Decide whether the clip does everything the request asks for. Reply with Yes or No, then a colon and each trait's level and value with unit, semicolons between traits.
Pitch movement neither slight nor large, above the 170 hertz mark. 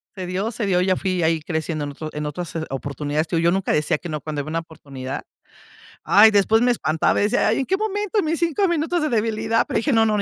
No: wide, 6.6 semitones; medium, 185 Hz